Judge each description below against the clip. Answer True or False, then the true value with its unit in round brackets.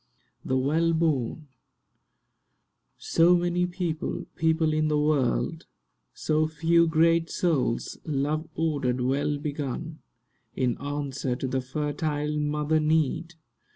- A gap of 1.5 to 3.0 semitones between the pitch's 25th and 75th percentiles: True (2.4 semitones)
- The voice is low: False (155 Hz)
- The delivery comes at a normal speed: False (100 wpm)